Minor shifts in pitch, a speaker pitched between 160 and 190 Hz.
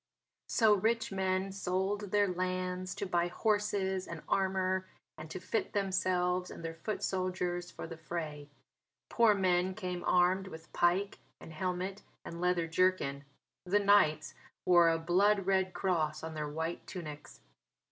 Yes: narrow, 2.1 semitones; medium, 185 Hz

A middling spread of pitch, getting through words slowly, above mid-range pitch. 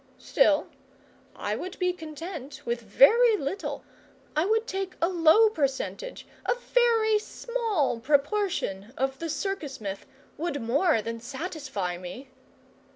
No: wide, 7.4 semitones; slow, 125 wpm; very high, 315 Hz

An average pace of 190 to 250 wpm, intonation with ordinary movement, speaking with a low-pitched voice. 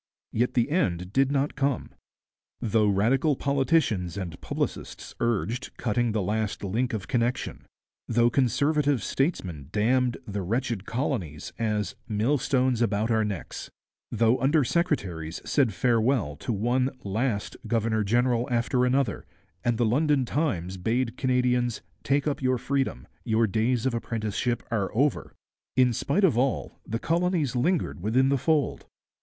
No: average, 140 wpm; average, 3.9 semitones; low, 120 Hz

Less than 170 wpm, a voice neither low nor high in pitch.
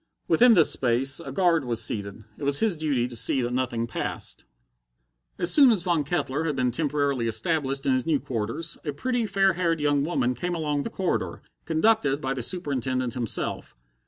No: average, 190 wpm; medium, 145 Hz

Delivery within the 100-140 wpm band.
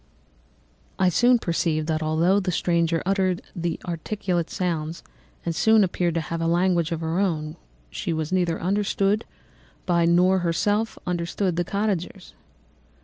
Yes: slow, 135 wpm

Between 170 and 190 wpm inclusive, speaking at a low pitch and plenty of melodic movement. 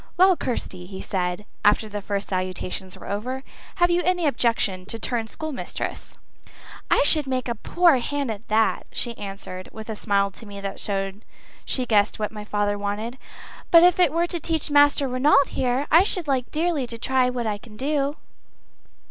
No: average, 185 wpm; high, 235 Hz; wide, 6.0 semitones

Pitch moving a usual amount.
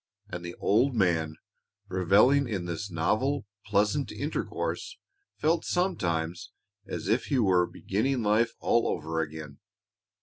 No: wide, 7.2 semitones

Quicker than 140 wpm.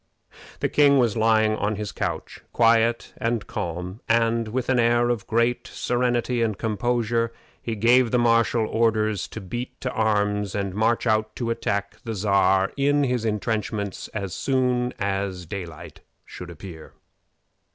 Yes: average, 150 wpm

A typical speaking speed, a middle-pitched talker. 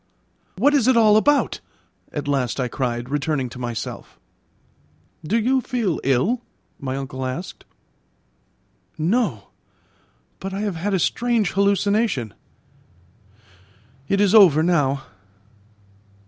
No: slow, 115 wpm; medium, 180 Hz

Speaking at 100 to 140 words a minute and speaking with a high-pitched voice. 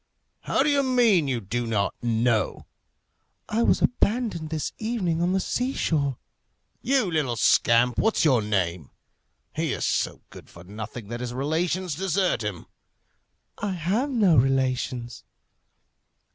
No: slow, 135 wpm; medium, 150 Hz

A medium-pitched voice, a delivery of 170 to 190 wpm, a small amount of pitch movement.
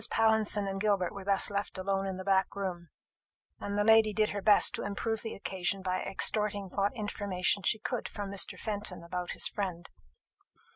No: high, 200 Hz; average, 185 wpm; narrow, 1.8 semitones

